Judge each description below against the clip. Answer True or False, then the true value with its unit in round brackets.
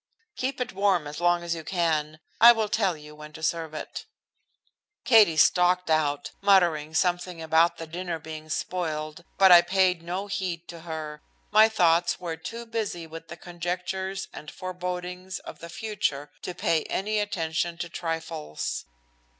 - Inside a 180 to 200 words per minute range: False (160 wpm)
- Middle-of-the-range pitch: True (175 Hz)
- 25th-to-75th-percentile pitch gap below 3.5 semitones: True (2.8 semitones)